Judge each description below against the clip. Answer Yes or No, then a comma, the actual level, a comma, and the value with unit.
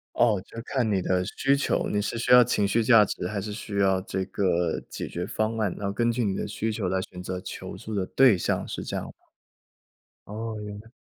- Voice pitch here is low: Yes, low, 105 Hz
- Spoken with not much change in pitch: No, average, 3.2 semitones